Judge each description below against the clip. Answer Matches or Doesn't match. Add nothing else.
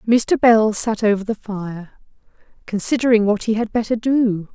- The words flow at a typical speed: Matches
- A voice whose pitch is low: Doesn't match